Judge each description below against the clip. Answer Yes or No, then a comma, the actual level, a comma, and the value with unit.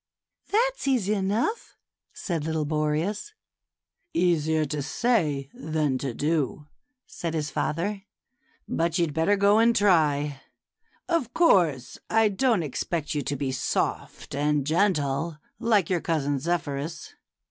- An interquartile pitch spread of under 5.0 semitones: No, wide, 5.6 semitones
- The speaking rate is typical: No, slow, 130 wpm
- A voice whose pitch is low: No, medium, 160 Hz